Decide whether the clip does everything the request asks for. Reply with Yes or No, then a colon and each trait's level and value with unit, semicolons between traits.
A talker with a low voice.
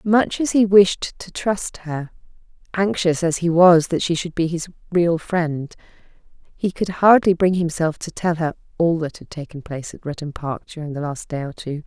No: medium, 170 Hz